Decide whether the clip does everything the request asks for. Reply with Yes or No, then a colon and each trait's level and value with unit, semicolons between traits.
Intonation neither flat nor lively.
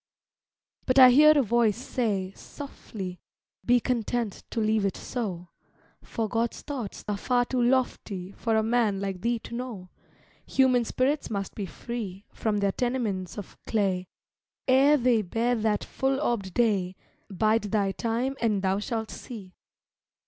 Yes: average, 3.7 semitones